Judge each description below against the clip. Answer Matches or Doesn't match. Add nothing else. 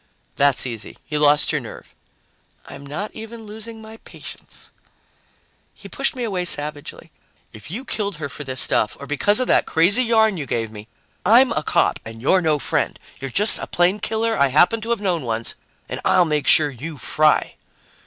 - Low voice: Doesn't match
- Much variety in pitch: Matches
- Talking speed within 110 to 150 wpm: Doesn't match